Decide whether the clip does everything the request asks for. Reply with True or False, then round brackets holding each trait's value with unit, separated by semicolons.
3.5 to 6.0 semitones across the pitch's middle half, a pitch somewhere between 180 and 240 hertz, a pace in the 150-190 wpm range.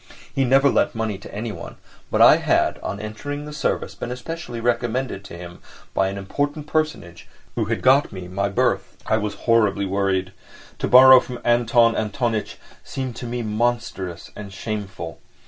False (4.1 semitones; 115 Hz; 165 wpm)